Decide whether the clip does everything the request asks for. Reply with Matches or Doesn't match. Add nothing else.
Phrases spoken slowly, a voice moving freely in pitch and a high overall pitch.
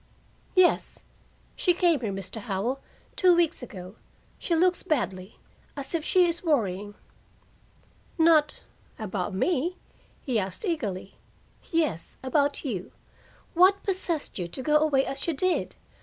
Matches